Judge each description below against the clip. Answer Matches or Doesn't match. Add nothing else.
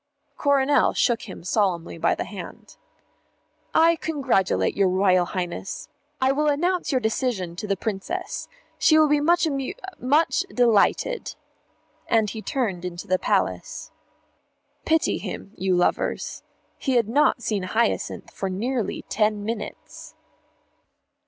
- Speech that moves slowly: Matches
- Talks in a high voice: Matches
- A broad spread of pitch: Matches